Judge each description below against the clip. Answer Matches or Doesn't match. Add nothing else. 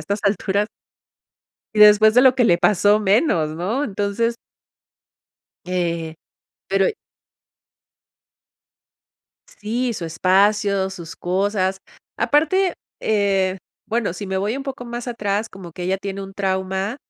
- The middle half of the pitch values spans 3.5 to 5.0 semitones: Doesn't match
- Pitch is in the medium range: Doesn't match